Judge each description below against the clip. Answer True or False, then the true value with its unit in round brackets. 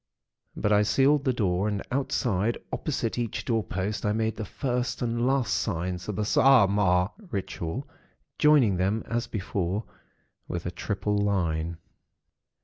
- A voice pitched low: True (105 Hz)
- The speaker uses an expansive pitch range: False (4.2 semitones)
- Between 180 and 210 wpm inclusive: False (140 wpm)